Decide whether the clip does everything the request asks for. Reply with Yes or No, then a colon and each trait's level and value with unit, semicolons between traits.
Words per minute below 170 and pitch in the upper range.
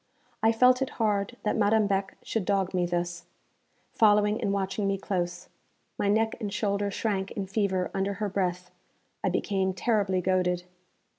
Yes: average, 160 wpm; high, 200 Hz